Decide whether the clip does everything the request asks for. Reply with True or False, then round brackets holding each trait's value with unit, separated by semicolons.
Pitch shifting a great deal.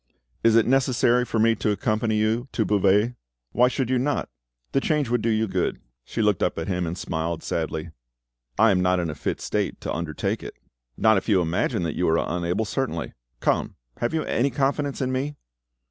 True (5.7 semitones)